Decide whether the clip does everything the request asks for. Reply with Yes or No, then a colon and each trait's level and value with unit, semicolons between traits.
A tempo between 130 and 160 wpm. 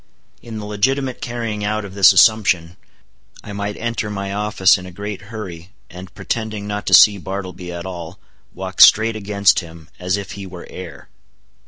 No: average, 175 wpm